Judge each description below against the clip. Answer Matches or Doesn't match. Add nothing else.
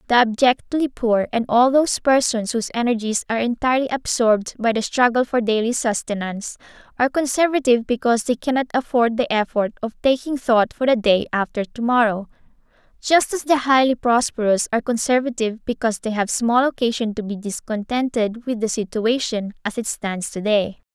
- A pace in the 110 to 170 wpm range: Matches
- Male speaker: Doesn't match